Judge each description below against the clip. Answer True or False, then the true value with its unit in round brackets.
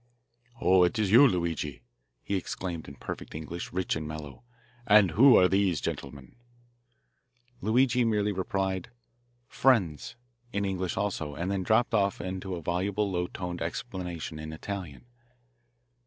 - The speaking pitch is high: False (95 Hz)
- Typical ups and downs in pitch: True (3.4 semitones)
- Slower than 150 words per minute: True (140 wpm)